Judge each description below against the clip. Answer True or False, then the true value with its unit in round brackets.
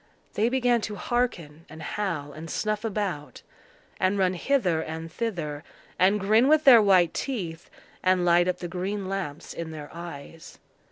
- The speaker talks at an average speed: True (160 wpm)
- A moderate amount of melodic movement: True (4.5 semitones)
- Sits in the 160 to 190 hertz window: True (185 Hz)